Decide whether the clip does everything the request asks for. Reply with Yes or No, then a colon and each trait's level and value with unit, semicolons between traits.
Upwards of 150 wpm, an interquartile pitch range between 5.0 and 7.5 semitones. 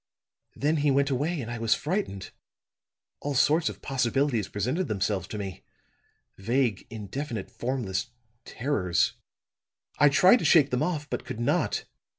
No: average, 145 wpm; average, 5.3 semitones